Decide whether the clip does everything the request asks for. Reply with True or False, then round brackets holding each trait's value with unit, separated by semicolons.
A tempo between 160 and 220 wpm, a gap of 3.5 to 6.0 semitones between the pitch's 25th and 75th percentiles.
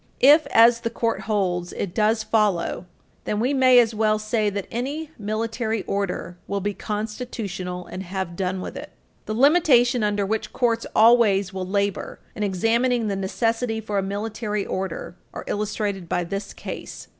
False (165 wpm; 2.8 semitones)